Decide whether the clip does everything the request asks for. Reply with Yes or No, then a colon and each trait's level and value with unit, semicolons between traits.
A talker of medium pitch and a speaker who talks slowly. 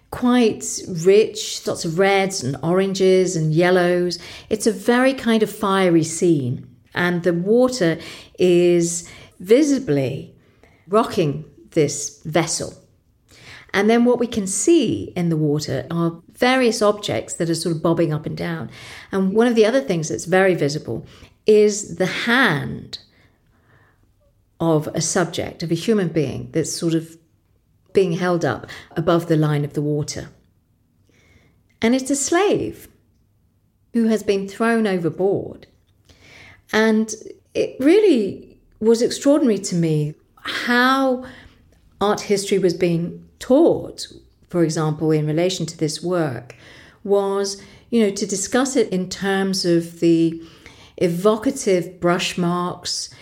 Yes: medium, 180 Hz; slow, 130 wpm